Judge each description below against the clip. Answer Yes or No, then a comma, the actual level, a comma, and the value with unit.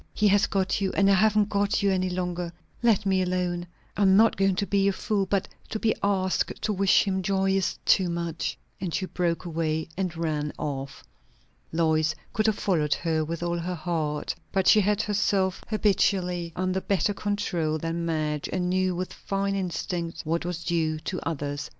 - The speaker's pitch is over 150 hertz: Yes, medium, 185 Hz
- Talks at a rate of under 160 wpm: No, average, 190 wpm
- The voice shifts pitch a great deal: No, average, 2.9 semitones